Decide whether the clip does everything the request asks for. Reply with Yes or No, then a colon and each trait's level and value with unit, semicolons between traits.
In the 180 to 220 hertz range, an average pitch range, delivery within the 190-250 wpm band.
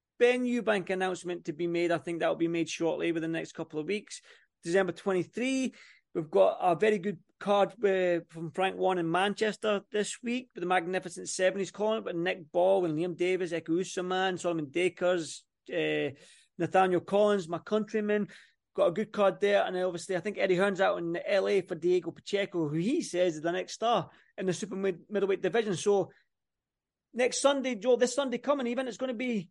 Yes: high, 190 Hz; average, 3.2 semitones; average, 200 wpm